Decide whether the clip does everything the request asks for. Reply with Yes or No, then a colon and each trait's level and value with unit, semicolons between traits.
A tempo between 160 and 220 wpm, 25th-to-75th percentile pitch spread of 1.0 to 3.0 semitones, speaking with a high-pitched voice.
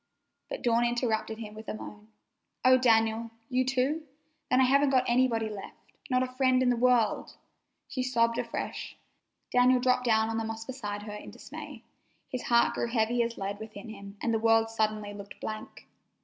Yes: average, 190 wpm; narrow, 2.5 semitones; high, 230 Hz